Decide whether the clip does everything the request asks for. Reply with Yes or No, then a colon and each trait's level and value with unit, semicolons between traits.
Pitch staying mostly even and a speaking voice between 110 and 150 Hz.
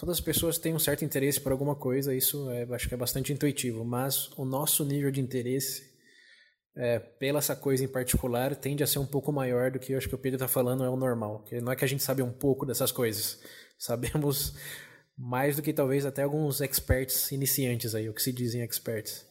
Yes: narrow, 2.2 semitones; low, 135 Hz